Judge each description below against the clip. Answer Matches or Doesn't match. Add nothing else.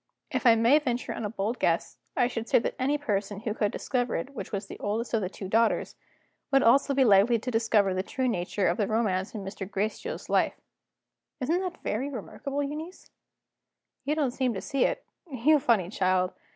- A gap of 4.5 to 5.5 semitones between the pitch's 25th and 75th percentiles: Matches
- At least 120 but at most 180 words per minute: Doesn't match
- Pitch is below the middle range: Doesn't match